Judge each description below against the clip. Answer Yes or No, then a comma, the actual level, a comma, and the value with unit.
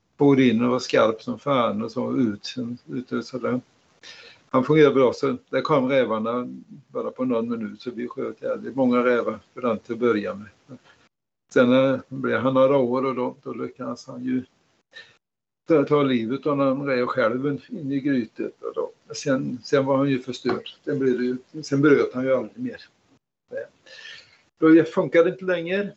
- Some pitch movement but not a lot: Yes, average, 3.9 semitones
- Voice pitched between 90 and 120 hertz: No, low, 130 Hz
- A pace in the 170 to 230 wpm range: Yes, average, 175 wpm